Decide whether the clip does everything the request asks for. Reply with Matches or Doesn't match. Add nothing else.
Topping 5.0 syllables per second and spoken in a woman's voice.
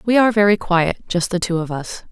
Matches